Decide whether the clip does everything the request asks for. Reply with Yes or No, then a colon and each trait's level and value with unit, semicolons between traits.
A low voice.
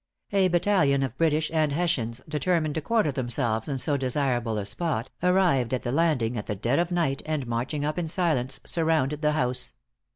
No: medium, 145 Hz